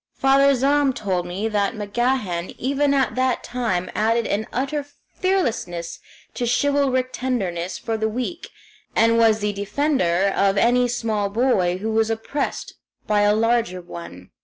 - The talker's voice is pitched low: No, high, 225 Hz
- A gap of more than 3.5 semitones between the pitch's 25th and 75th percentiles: Yes, average, 4.5 semitones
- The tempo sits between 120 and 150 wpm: Yes, average, 145 wpm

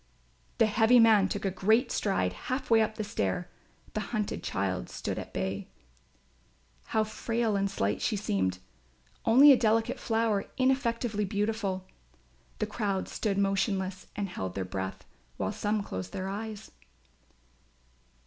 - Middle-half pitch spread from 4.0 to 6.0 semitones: No, average, 3.1 semitones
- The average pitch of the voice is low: No, high, 205 Hz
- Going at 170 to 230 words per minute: No, average, 140 wpm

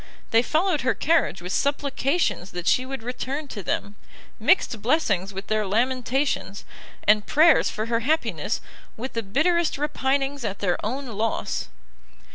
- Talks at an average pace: Yes, average, 145 wpm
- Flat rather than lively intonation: No, average, 5.2 semitones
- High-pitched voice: Yes, very high, 250 Hz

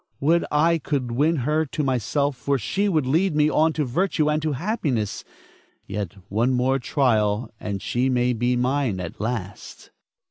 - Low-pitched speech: Yes, low, 130 Hz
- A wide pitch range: No, average, 4.1 semitones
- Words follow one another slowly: No, average, 170 wpm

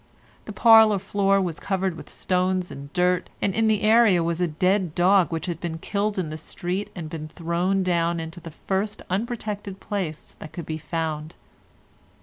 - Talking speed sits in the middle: Yes, average, 180 wpm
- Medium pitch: Yes, medium, 180 Hz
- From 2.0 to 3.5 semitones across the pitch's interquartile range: Yes, average, 3.2 semitones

